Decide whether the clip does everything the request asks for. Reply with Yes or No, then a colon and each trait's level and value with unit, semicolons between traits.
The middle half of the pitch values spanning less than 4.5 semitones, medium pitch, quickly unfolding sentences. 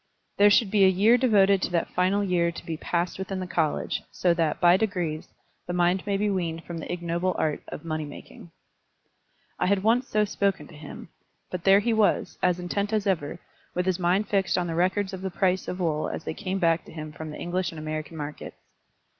Yes: average, 2.8 semitones; medium, 180 Hz; fast, 220 wpm